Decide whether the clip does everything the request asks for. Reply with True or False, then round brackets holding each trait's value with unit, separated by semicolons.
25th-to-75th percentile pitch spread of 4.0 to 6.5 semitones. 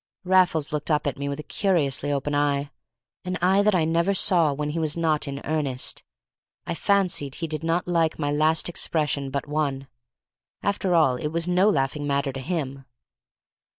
False (3.2 semitones)